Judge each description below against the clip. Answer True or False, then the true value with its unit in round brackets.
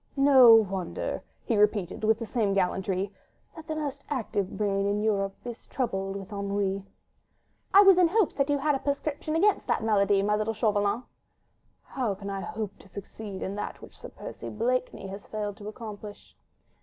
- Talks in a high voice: True (210 Hz)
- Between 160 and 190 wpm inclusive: True (180 wpm)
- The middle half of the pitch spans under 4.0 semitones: False (4.3 semitones)